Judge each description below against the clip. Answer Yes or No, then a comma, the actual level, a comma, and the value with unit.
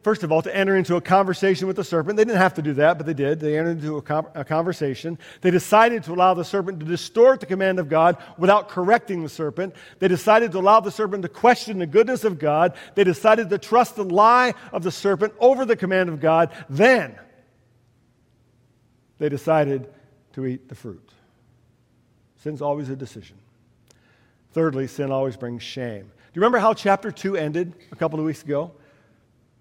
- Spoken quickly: No, average, 195 wpm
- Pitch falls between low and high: Yes, medium, 165 Hz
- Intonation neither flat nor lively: No, wide, 6.5 semitones